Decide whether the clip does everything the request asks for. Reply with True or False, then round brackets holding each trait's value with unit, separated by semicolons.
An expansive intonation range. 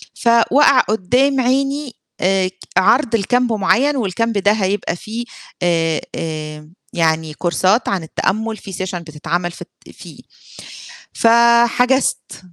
True (5.9 semitones)